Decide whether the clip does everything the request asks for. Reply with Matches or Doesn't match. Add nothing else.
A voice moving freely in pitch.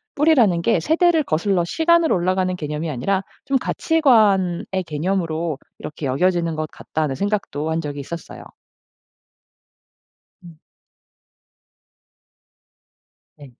Doesn't match